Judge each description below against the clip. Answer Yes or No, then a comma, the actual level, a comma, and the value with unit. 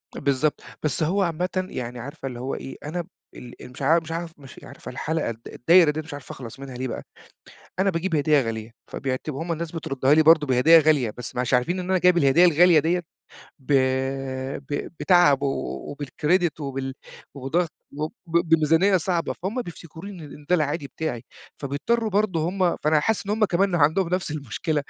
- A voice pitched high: No, medium, 155 Hz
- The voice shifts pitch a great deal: No, average, 4.2 semitones